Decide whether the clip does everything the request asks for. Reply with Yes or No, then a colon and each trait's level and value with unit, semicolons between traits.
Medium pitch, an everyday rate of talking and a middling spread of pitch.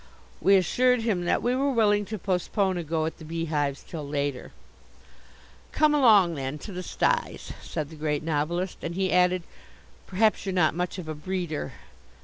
Yes: medium, 180 Hz; average, 175 wpm; average, 4.2 semitones